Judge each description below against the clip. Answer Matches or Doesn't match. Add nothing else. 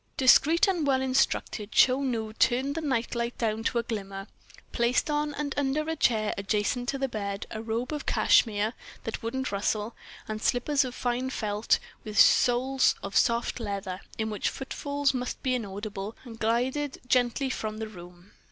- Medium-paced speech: Matches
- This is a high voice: Matches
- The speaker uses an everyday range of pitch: Matches